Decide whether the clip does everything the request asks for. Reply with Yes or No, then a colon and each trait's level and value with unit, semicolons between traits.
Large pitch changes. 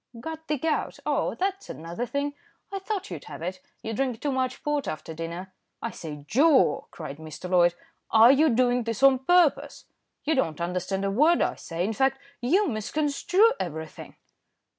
Yes: wide, 8.8 semitones